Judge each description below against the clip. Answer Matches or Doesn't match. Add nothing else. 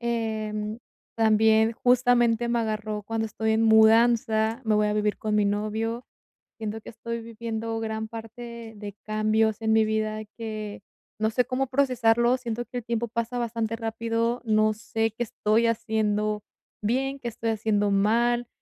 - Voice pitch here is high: Matches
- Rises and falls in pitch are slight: Matches